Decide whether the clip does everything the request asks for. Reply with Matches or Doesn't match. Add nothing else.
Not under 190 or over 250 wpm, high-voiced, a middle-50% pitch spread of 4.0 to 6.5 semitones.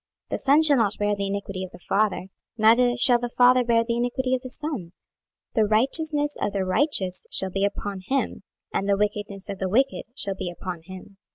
Matches